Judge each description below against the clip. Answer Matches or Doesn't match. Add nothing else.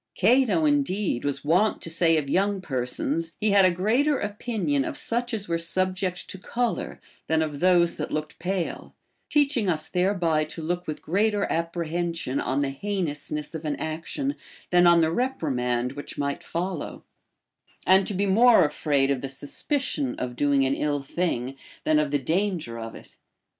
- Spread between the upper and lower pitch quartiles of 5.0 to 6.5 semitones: Matches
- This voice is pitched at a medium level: Matches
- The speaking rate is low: Doesn't match